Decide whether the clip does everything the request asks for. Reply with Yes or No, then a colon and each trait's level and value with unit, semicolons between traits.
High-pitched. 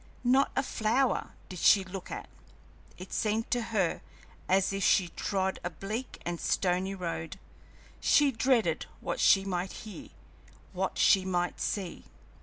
Yes: high, 195 Hz